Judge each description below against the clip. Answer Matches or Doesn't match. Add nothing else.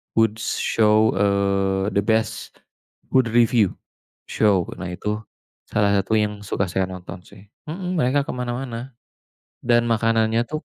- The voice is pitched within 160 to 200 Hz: Doesn't match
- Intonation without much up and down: Doesn't match